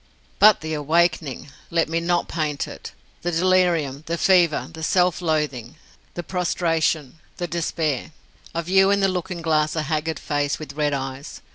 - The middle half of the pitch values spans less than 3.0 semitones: Yes, narrow, 2.6 semitones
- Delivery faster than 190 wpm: No, average, 160 wpm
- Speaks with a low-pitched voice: No, medium, 160 Hz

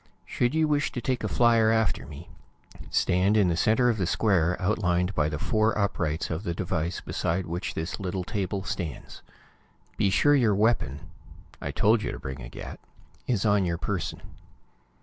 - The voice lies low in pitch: Yes, very low, 95 Hz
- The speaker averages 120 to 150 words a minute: No, average, 180 wpm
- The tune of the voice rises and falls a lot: No, average, 4.5 semitones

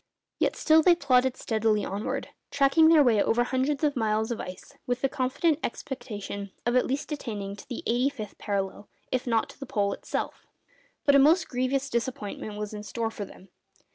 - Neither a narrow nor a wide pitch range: Yes, average, 4.5 semitones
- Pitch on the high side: Yes, high, 245 Hz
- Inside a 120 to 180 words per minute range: No, average, 190 wpm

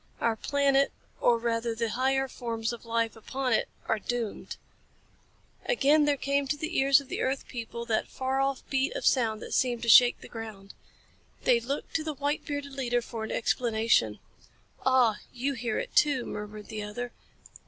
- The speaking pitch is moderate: No, high, 245 Hz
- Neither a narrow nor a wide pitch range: Yes, average, 3.2 semitones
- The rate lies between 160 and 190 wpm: Yes, average, 175 wpm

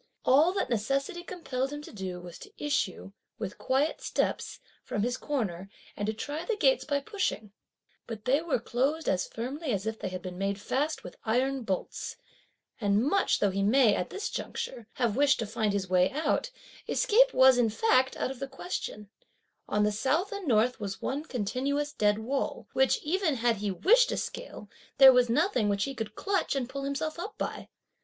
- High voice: Yes, very high, 255 Hz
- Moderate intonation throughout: No, wide, 6.0 semitones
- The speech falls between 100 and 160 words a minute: No, average, 195 wpm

